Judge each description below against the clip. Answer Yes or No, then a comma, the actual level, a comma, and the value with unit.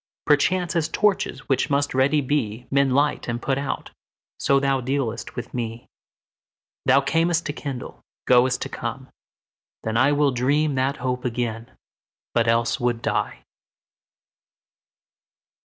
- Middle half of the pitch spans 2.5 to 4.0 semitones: Yes, average, 3.0 semitones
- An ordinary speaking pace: No, slow, 120 wpm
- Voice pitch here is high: No, low, 135 Hz